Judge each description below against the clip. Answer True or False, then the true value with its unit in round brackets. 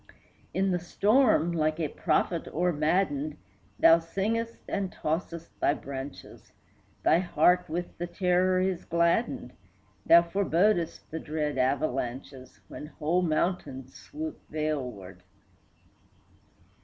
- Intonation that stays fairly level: False (3.4 semitones)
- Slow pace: True (105 wpm)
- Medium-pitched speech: True (165 Hz)